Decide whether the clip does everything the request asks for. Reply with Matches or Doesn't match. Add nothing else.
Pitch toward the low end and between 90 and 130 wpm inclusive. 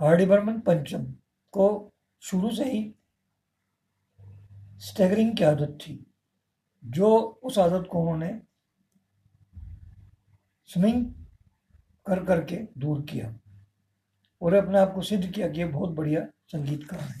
Doesn't match